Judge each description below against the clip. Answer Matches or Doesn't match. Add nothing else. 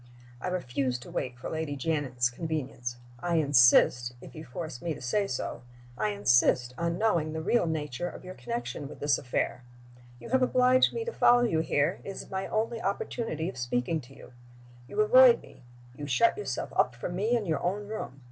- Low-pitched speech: Doesn't match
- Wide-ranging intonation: Matches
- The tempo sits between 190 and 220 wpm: Matches